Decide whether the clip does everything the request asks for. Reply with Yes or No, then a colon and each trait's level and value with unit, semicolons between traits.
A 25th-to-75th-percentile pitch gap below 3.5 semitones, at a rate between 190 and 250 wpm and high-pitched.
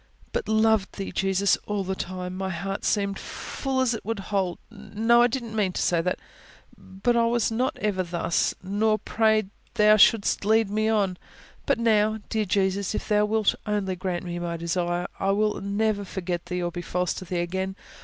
Yes: average, 2.9 semitones; average, 195 wpm; high, 200 Hz